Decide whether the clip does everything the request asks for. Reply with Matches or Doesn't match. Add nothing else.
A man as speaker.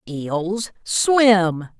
Doesn't match